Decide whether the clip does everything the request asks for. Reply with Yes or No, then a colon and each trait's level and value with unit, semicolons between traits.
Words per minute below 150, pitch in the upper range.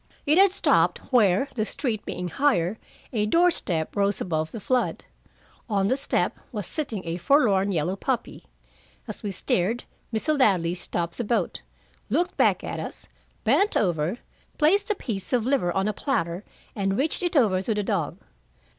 No: average, 170 wpm; high, 210 Hz